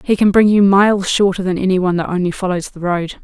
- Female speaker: Yes, female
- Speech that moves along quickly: Yes, fast, 260 wpm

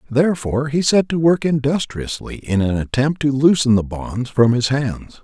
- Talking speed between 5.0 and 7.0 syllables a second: No, 4.8 syllables/s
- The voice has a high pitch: No, low, 135 Hz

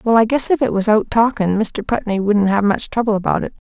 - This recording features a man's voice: No, female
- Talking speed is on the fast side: Yes, fast, 260 wpm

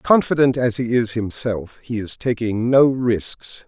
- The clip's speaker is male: Yes, male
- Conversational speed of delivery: Yes, average, 165 wpm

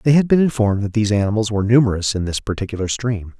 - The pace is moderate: No, fast, 230 wpm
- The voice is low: Yes, low, 110 Hz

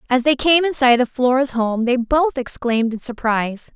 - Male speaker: No, female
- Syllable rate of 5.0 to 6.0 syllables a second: Yes, 5.1 syllables/s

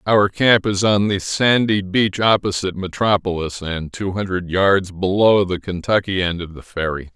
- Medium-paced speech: Yes, average, 170 wpm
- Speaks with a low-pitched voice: Yes, very low, 95 Hz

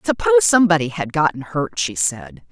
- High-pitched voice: No, medium, 145 Hz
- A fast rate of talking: No, average, 165 wpm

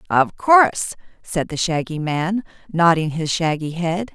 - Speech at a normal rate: Yes, average, 145 wpm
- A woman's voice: Yes, female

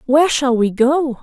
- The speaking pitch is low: No, very high, 270 Hz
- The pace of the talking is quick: No, average, 195 wpm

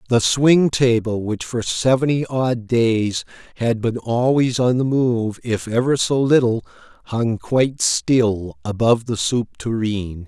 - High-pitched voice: No, low, 120 Hz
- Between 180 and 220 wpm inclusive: No, average, 145 wpm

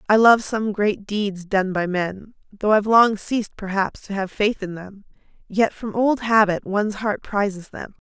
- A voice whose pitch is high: Yes, high, 205 Hz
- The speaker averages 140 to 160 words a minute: No, average, 195 wpm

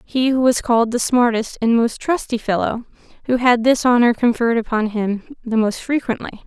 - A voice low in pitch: No, high, 235 Hz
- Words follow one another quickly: No, average, 175 wpm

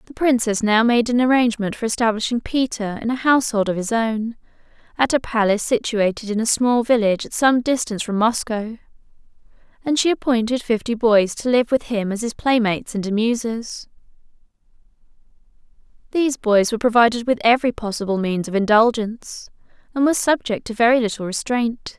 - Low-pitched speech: No, high, 230 Hz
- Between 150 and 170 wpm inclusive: Yes, average, 160 wpm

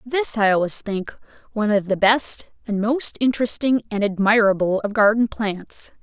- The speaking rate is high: No, average, 160 wpm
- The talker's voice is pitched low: No, high, 215 Hz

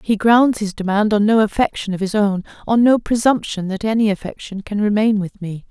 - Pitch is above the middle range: Yes, high, 210 Hz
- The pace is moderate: No, fast, 210 wpm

